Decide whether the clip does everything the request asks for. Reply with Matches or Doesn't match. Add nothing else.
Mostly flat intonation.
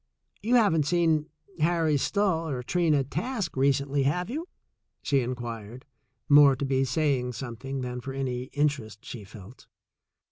Doesn't match